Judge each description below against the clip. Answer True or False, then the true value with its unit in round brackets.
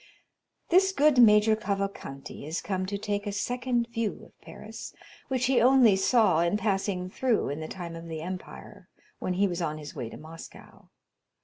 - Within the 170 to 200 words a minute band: True (180 wpm)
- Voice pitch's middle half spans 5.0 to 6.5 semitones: True (5.4 semitones)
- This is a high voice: True (200 Hz)